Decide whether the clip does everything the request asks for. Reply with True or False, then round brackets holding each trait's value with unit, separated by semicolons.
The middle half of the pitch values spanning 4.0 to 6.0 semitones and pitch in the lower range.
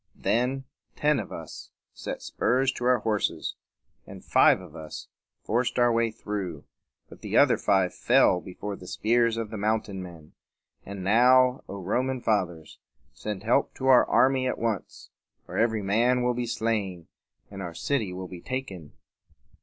True (4.5 semitones; 110 Hz)